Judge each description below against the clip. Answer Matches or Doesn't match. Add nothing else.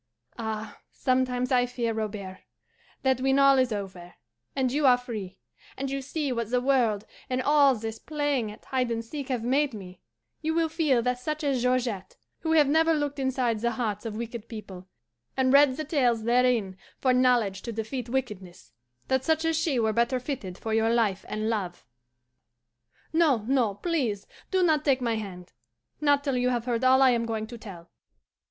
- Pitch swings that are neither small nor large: Matches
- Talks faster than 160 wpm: Matches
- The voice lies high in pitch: Matches